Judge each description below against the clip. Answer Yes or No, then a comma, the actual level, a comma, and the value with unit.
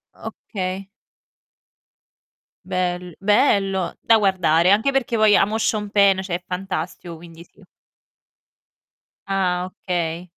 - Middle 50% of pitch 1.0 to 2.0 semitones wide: No, narrow, 2.5 semitones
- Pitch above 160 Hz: Yes, high, 190 Hz